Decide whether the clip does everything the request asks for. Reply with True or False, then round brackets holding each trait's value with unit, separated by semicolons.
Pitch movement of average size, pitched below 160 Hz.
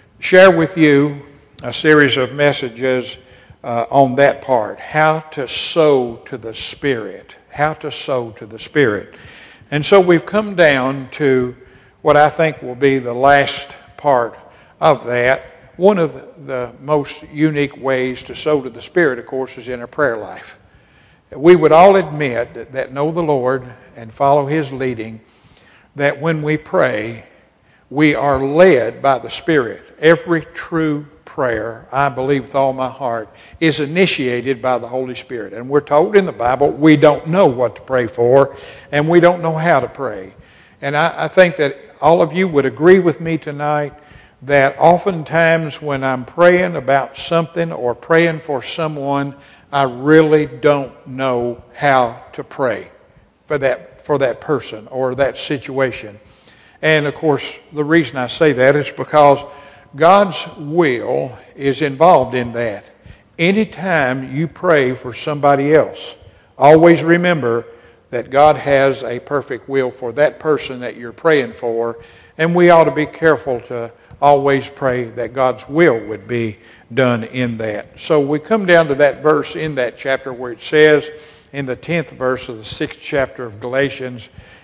True (3.5 semitones; 140 Hz)